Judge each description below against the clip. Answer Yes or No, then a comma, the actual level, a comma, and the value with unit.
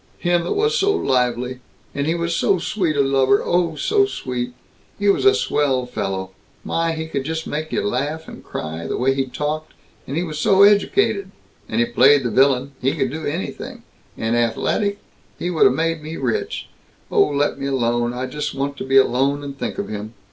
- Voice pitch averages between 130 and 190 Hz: Yes, medium, 140 Hz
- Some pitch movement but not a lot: Yes, average, 4.6 semitones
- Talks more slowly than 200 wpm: No, fast, 205 wpm